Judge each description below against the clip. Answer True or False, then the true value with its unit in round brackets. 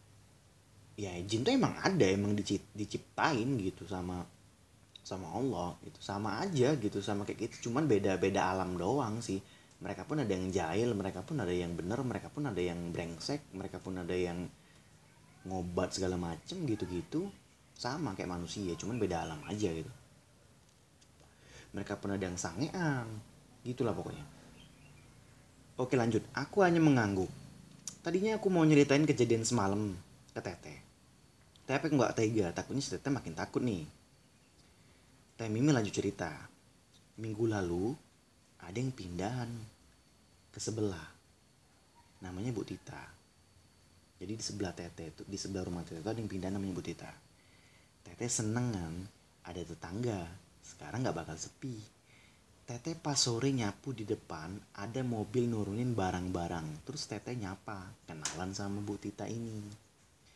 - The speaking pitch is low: True (100 Hz)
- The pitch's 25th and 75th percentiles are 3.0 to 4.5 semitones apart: False (5.0 semitones)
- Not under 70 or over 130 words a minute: False (140 wpm)